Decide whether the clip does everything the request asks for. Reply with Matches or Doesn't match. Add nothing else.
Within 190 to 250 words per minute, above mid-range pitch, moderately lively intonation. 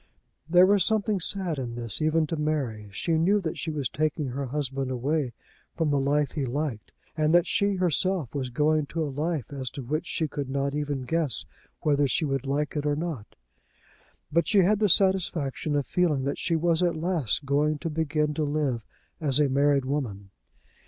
Doesn't match